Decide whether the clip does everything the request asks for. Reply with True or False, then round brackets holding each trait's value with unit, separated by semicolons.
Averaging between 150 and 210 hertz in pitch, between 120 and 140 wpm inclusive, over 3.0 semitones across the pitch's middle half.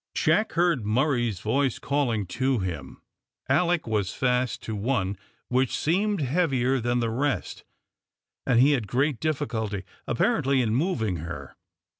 False (125 Hz; 135 wpm; 4.8 semitones)